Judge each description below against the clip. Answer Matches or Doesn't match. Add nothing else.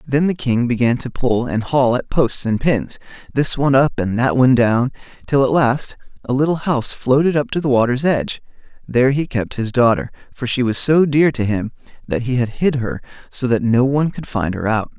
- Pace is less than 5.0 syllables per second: Doesn't match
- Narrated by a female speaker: Doesn't match